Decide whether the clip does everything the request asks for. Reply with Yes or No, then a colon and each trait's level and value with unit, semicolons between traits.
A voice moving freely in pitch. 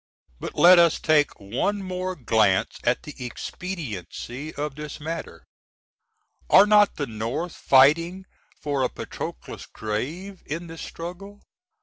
Yes: wide, 6.3 semitones